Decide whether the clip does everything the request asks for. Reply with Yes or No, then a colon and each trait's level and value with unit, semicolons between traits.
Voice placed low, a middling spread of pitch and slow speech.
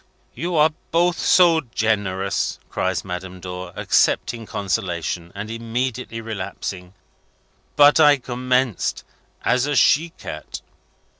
No: low, 115 Hz; wide, 6.8 semitones; slow, 105 wpm